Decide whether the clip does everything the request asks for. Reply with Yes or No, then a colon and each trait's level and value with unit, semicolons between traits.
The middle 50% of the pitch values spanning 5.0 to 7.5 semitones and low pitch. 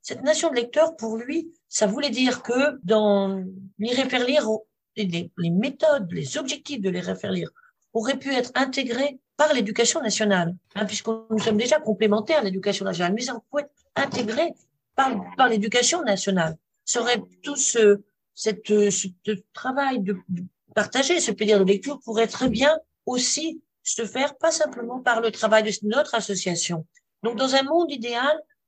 No: average, 5.3 semitones; high, 235 Hz